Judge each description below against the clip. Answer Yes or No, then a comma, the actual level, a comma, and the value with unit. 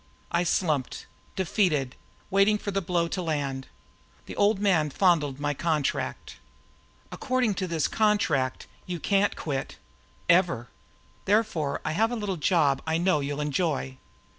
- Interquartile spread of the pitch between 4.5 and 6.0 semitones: Yes, average, 5.2 semitones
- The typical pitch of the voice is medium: Yes, medium, 170 Hz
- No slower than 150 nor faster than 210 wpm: No, average, 140 wpm